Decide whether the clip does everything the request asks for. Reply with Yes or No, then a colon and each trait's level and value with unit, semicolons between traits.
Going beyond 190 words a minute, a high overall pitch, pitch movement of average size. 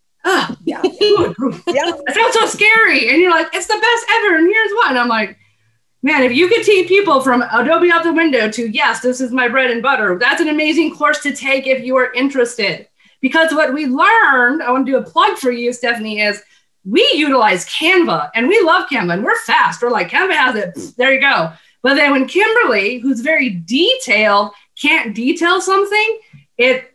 No: fast, 205 wpm; very high, 275 Hz; wide, 7.0 semitones